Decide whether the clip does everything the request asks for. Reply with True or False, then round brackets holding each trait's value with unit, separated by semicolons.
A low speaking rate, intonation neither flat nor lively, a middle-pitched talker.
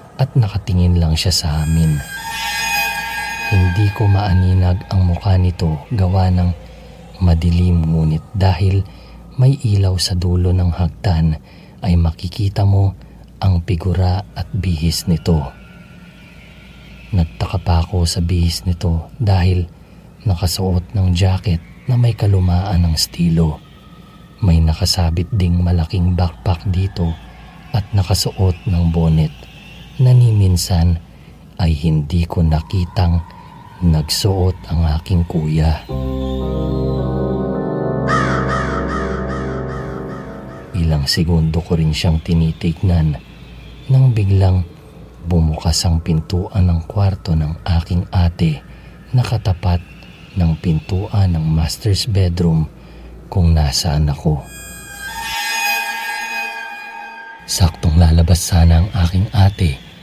False (95 wpm; 3.1 semitones; 90 Hz)